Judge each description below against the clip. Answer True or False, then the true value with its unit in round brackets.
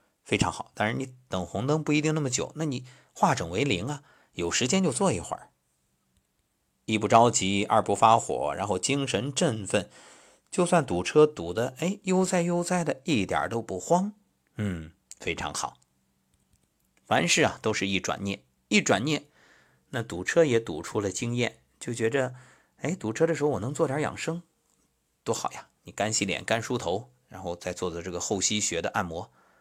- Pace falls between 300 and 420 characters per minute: False (250 characters per minute)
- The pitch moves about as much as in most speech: False (8.0 semitones)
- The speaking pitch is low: True (120 Hz)